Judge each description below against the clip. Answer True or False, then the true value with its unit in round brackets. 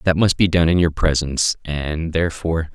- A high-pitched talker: False (80 Hz)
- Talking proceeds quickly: False (195 wpm)